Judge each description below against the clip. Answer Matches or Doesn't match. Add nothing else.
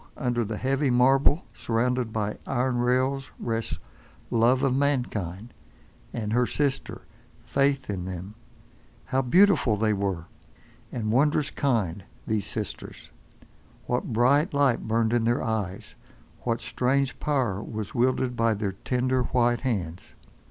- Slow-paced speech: Matches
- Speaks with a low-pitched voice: Matches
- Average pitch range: Matches